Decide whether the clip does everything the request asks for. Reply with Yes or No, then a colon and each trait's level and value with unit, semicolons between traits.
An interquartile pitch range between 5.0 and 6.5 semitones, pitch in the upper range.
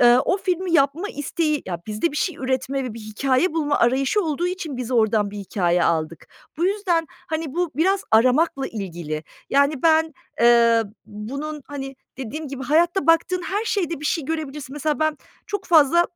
Yes: wide, 5.5 semitones; very high, 285 Hz